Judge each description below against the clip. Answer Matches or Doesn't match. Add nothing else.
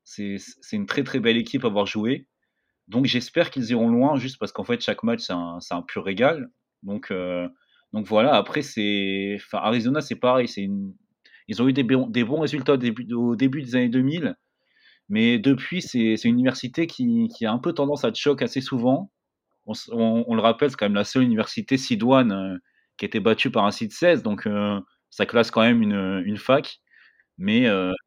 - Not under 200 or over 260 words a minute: Matches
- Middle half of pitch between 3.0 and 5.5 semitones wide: Matches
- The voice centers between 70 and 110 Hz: Doesn't match